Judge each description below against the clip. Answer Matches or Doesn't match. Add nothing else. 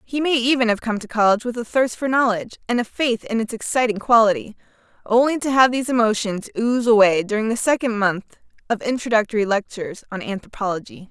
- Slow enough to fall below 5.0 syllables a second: Doesn't match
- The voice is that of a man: Doesn't match